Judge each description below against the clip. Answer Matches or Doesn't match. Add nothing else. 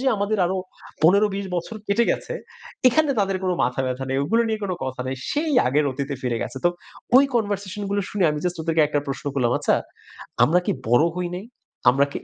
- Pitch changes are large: Matches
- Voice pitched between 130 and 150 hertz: Doesn't match